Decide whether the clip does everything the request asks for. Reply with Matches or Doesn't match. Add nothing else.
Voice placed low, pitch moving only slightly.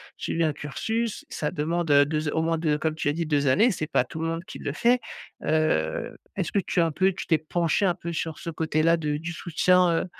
Doesn't match